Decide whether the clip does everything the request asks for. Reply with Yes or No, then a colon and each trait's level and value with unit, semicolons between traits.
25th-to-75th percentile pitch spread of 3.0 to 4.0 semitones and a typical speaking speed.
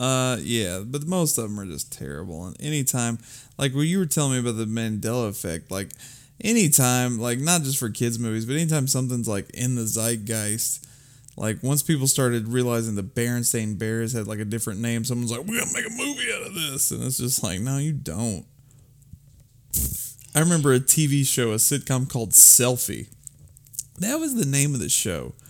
Yes: average, 3.5 semitones; average, 195 wpm